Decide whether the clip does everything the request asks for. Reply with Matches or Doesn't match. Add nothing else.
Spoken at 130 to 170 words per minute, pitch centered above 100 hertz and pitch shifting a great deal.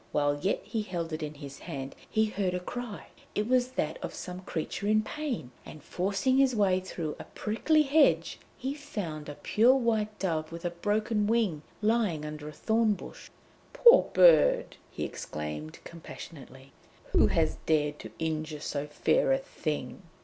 Matches